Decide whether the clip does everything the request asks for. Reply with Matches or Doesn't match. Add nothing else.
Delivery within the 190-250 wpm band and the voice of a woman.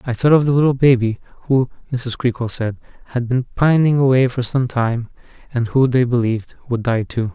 Doesn't match